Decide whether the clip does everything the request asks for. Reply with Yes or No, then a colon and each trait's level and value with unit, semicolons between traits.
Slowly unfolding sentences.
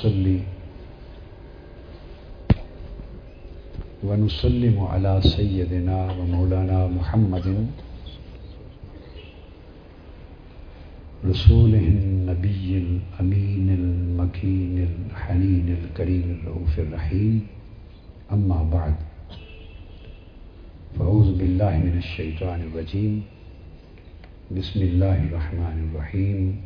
Yes: slow, 55 wpm